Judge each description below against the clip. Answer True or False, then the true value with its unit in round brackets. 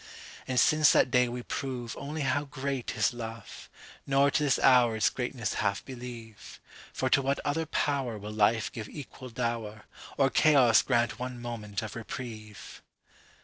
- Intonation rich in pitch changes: False (3.3 semitones)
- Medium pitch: False (125 Hz)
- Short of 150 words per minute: True (140 wpm)